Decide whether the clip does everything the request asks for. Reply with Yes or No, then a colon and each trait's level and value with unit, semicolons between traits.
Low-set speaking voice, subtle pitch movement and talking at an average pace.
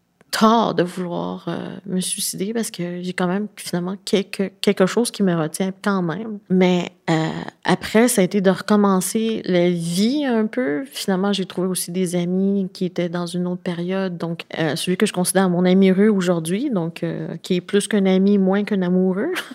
No: medium, 185 Hz; narrow, 2.2 semitones; average, 195 wpm